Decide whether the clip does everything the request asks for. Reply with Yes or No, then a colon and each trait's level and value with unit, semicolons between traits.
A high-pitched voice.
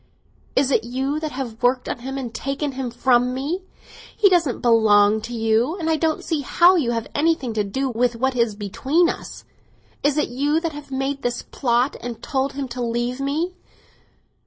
Yes: very high, 265 Hz